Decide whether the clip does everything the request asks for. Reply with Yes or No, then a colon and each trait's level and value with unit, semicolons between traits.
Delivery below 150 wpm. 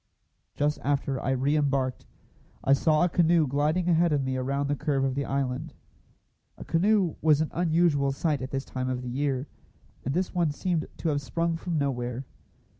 No: average, 190 wpm